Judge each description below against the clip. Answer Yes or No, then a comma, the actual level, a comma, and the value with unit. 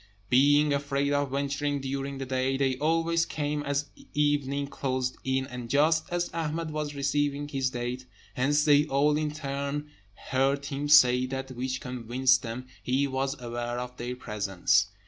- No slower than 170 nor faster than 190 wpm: No, average, 160 wpm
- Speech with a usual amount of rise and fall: No, narrow, 2.2 semitones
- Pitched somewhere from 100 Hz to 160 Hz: Yes, medium, 140 Hz